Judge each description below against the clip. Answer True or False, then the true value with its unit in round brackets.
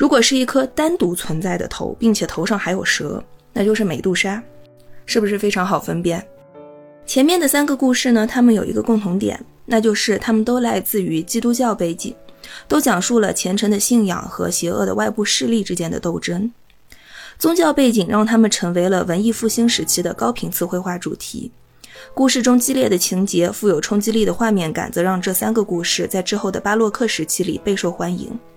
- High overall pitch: True (210 Hz)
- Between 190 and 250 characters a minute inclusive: False (305 characters per minute)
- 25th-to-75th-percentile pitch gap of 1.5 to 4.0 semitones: False (4.6 semitones)